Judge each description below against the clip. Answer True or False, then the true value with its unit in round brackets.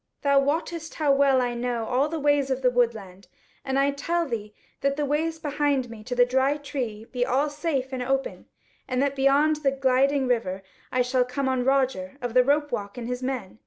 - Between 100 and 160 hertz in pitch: False (265 Hz)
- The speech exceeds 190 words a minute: True (205 wpm)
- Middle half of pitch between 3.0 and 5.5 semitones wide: False (2.4 semitones)